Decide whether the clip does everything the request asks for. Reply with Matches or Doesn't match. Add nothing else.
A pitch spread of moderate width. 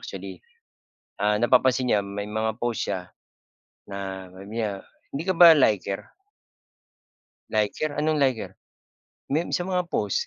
Doesn't match